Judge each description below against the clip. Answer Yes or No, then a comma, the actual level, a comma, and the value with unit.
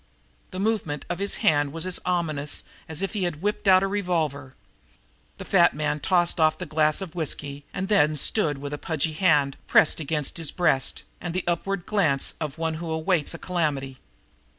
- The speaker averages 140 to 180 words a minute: No, average, 190 wpm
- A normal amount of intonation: Yes, average, 3.8 semitones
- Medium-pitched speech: Yes, medium, 160 Hz